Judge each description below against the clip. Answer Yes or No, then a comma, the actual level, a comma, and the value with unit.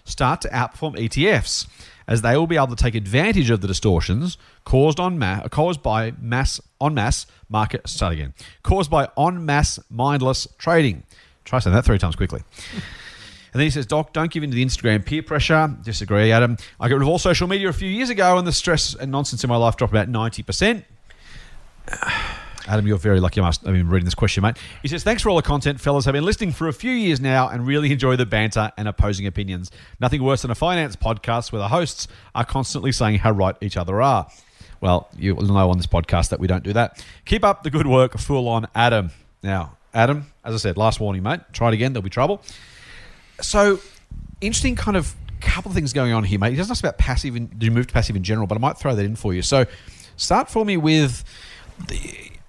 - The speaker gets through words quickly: Yes, fast, 225 wpm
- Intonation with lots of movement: Yes, wide, 6.1 semitones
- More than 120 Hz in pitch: No, low, 115 Hz